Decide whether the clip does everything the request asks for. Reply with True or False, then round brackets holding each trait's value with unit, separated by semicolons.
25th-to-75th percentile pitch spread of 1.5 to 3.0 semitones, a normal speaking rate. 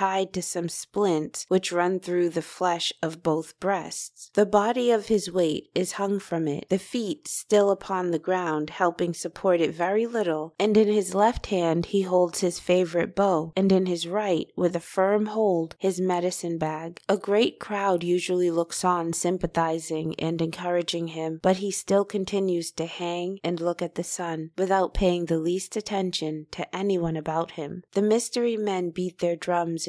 True (2.7 semitones; 180 wpm)